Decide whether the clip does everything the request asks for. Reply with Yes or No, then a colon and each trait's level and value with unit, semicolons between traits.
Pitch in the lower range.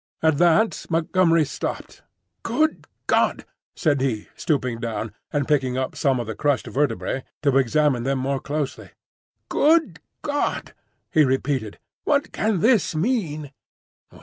No: medium, 145 Hz